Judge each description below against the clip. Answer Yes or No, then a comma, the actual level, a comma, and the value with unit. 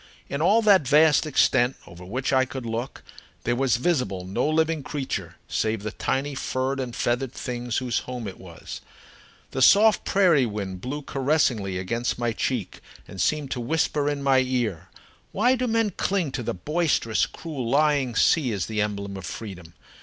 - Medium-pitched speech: No, low, 130 Hz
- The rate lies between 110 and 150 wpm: No, average, 175 wpm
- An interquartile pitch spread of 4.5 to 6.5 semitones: Yes, average, 5.0 semitones